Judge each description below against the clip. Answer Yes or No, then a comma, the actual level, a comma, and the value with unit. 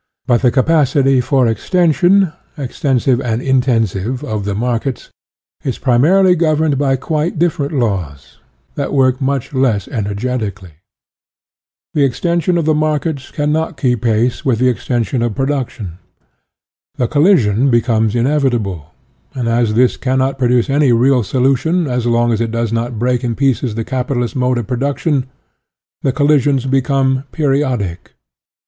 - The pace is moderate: Yes, average, 150 wpm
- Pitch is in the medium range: No, low, 130 Hz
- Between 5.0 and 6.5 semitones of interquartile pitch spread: No, average, 3.4 semitones